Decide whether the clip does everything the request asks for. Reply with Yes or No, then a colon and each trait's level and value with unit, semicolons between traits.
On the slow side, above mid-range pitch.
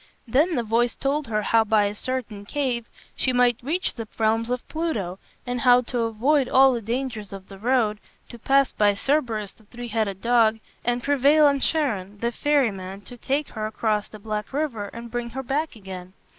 No: average, 195 wpm; high, 235 Hz